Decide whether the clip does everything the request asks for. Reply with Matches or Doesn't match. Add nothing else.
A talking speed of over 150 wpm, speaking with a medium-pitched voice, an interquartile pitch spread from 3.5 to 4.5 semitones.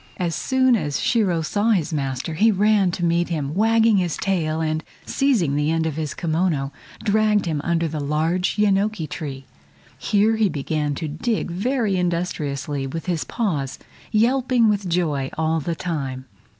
Doesn't match